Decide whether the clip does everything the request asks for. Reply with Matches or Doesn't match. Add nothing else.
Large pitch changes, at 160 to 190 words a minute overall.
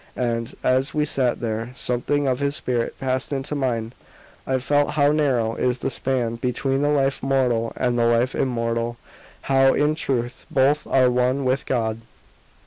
Doesn't match